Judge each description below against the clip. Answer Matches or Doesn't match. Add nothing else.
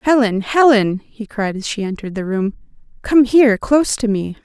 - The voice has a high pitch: Matches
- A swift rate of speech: Doesn't match